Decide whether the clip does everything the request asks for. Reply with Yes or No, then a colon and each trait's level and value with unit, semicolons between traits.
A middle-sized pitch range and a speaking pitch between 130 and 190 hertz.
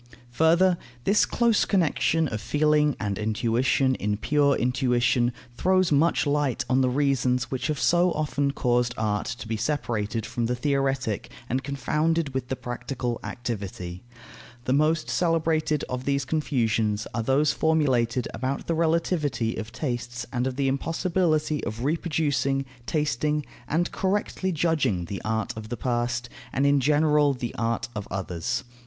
Yes: average, 4.2 semitones; low, 135 Hz